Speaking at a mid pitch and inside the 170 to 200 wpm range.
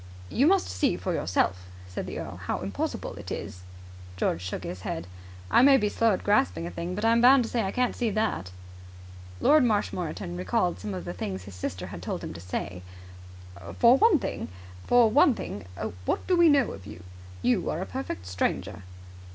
No: low, 105 Hz; average, 190 wpm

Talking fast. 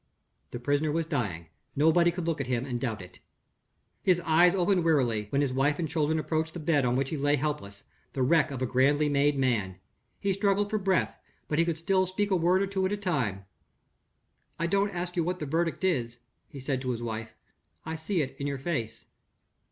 Yes: fast, 215 wpm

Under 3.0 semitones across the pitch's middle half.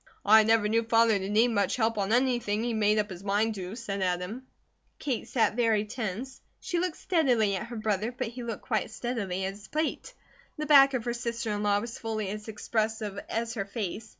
Yes: narrow, 2.5 semitones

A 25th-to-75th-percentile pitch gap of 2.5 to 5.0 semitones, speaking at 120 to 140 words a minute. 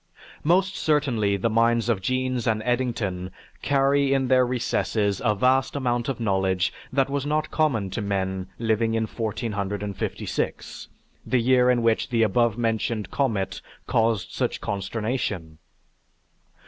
Yes: average, 4.0 semitones; slow, 135 wpm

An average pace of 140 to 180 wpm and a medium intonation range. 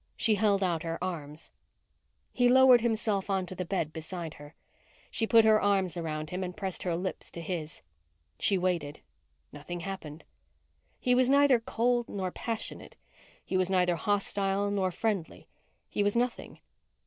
Yes: average, 155 wpm; average, 4.2 semitones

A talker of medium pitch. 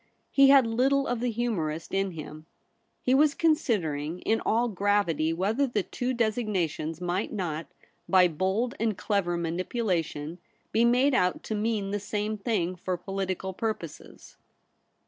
No: high, 200 Hz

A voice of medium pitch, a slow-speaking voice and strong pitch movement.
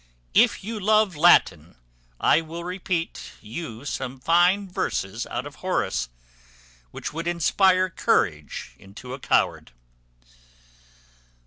Yes: medium, 165 Hz; slow, 110 wpm; wide, 7.3 semitones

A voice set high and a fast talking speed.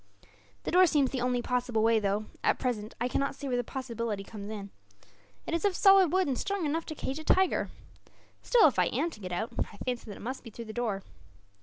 Yes: high, 245 Hz; fast, 240 wpm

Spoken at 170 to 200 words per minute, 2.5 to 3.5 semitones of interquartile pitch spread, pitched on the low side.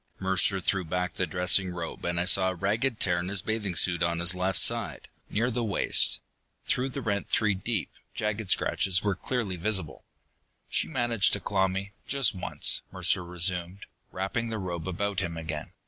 Yes: average, 180 wpm; average, 3.0 semitones; very low, 95 Hz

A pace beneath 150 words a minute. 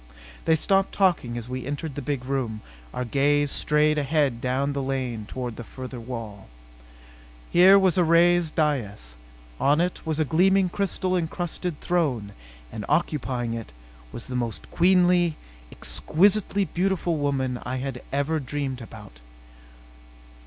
Yes: average, 140 wpm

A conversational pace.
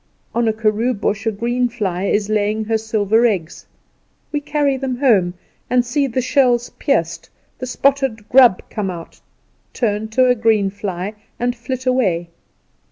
Yes: average, 160 wpm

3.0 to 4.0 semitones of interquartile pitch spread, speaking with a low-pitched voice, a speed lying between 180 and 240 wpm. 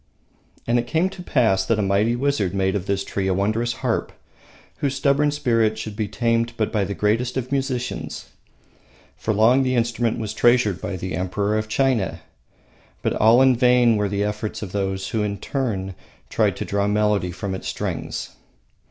Yes: average, 3.6 semitones; low, 110 Hz; average, 185 wpm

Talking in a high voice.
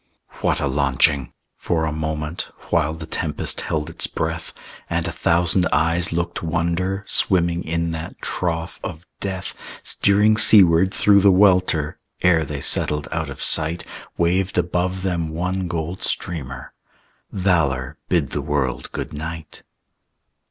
No: very low, 85 Hz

